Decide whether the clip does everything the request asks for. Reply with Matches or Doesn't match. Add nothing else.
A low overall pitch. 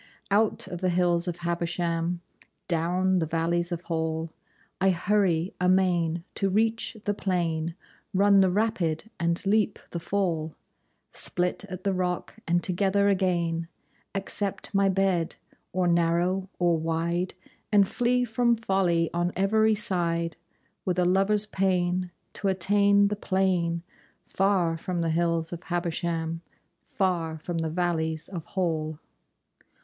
Doesn't match